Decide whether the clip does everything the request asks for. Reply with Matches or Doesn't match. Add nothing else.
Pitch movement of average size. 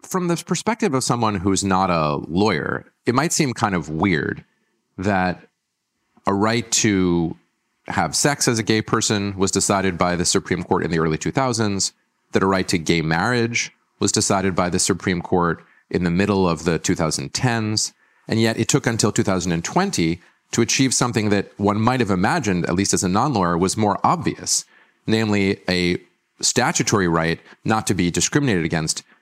Matches